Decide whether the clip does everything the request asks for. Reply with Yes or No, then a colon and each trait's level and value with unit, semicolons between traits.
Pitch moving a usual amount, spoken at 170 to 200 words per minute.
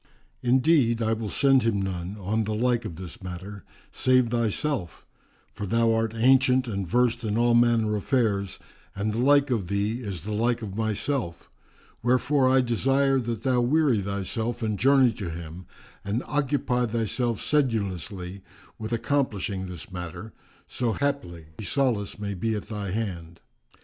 No: average, 4.0 semitones; average, 155 wpm